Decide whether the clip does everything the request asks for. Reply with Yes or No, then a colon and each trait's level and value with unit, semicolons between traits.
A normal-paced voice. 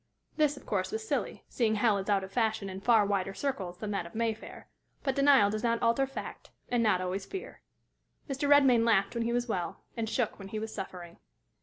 No: fast, 215 wpm